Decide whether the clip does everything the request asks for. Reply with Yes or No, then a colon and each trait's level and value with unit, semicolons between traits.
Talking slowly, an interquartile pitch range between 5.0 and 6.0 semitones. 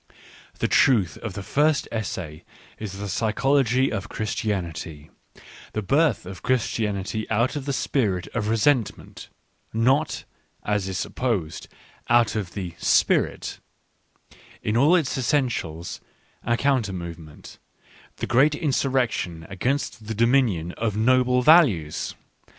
Yes: slow, 120 wpm; wide, 5.4 semitones